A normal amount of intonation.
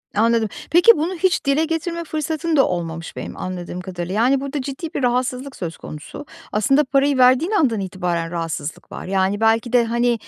No: wide, 7.8 semitones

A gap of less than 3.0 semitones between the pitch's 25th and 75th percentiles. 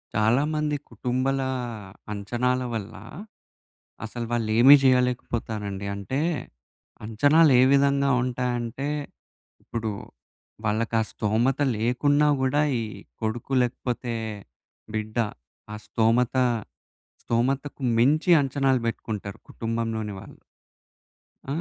No: average, 3.4 semitones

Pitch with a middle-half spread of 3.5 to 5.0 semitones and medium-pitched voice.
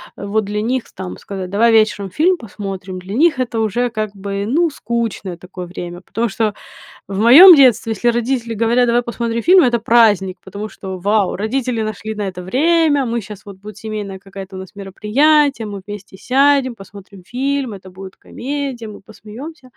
No: average, 4.0 semitones; high, 220 Hz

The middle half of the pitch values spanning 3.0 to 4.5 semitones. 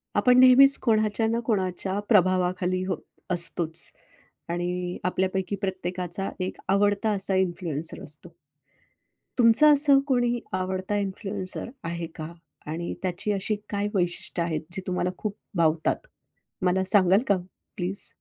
No: narrow, 2.6 semitones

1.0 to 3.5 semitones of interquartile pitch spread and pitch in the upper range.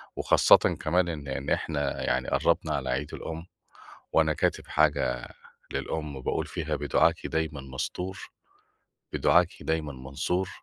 No: average, 3.2 semitones; very low, 75 Hz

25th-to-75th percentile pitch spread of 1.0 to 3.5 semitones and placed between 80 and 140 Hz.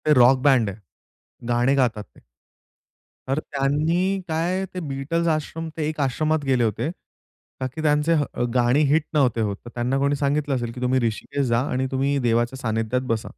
No: average, 3.9 semitones; low, 135 Hz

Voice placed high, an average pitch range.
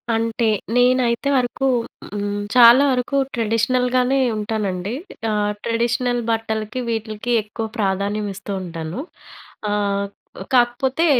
Yes: high, 230 Hz; average, 3.1 semitones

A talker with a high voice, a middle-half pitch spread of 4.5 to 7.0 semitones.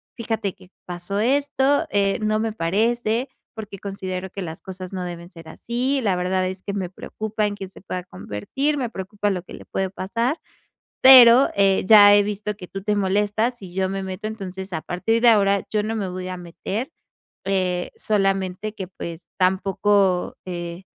No: high, 195 Hz; average, 2.8 semitones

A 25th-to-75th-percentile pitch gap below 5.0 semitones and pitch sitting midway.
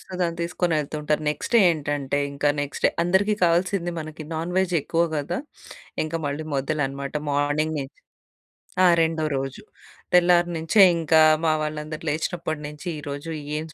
Yes: average, 2.7 semitones; medium, 155 Hz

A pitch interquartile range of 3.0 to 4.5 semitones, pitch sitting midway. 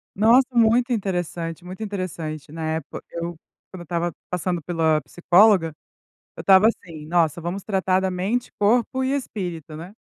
Yes: average, 3.9 semitones; medium, 180 Hz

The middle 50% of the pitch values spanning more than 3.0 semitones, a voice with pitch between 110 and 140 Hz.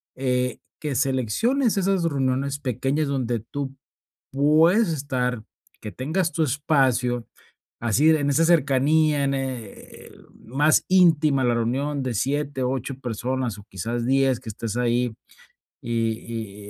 Yes: average, 3.5 semitones; low, 135 Hz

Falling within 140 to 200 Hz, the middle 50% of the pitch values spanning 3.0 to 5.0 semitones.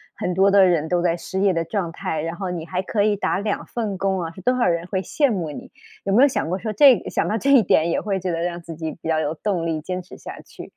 Yes: medium, 185 Hz; average, 3.3 semitones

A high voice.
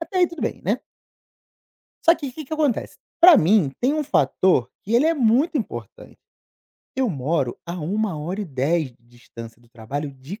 Yes: high, 195 Hz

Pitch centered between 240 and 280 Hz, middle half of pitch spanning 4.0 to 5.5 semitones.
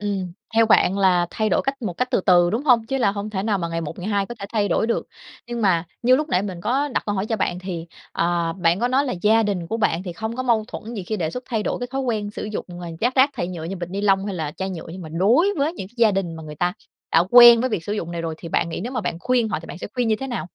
No: high, 205 Hz; average, 5.0 semitones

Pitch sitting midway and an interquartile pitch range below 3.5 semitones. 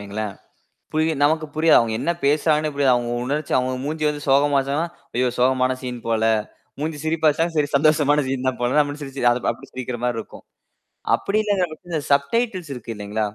No: medium, 145 Hz; average, 3.8 semitones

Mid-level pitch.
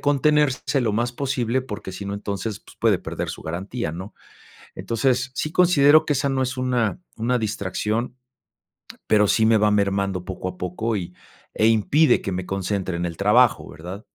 No: low, 110 Hz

